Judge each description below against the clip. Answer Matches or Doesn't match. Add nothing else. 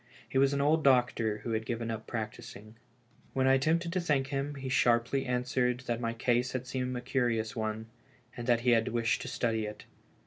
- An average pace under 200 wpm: Doesn't match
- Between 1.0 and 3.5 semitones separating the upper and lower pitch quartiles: Matches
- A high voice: Doesn't match